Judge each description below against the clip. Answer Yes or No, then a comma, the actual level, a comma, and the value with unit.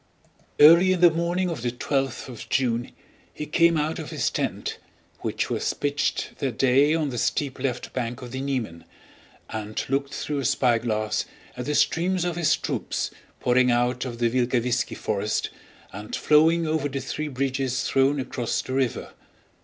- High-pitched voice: No, low, 135 Hz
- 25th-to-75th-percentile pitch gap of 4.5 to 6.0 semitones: No, average, 3.7 semitones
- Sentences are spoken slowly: No, average, 170 wpm